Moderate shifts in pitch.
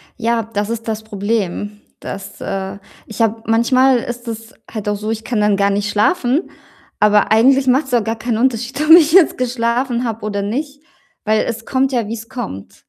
Yes: average, 3.1 semitones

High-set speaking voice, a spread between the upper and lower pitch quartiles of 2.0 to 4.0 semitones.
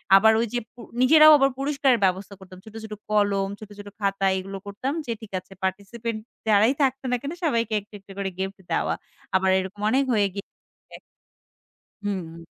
Yes: high, 205 Hz; average, 3.4 semitones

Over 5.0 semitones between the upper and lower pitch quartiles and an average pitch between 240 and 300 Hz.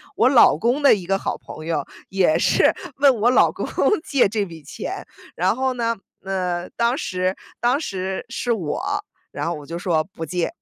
No: wide, 5.6 semitones; high, 190 Hz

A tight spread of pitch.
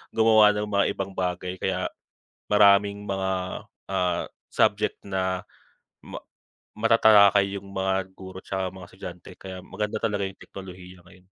Yes: narrow, 1.7 semitones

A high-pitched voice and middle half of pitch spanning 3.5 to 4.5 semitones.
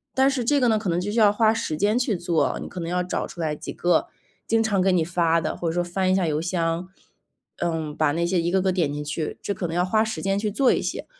No: medium, 180 Hz; average, 3.8 semitones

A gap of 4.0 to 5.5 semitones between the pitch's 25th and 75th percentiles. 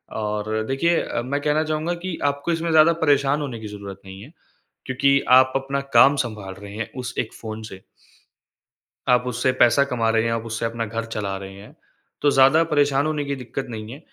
Yes: average, 4.6 semitones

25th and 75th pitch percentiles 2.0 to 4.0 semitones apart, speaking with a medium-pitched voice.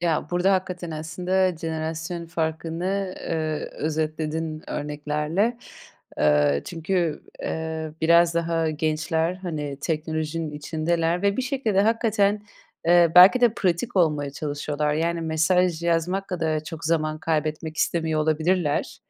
Yes: narrow, 2.4 semitones; medium, 165 Hz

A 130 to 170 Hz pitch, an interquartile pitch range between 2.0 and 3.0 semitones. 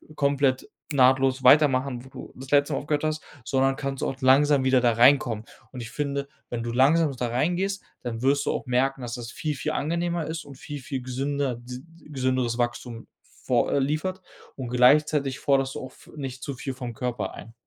Yes: low, 135 Hz; narrow, 2.5 semitones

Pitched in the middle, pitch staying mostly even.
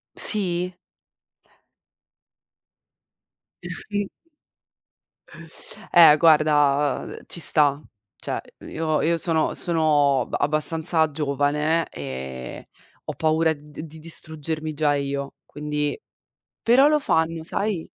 Yes: medium, 155 Hz; narrow, 2.2 semitones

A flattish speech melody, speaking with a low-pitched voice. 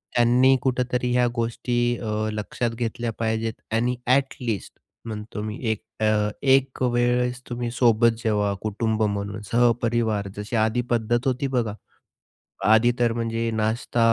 Yes: narrow, 1.9 semitones; low, 115 Hz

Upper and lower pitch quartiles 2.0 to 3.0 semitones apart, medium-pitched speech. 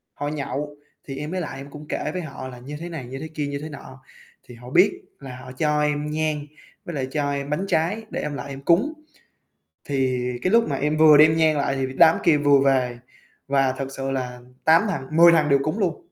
Yes: average, 2.7 semitones; medium, 145 Hz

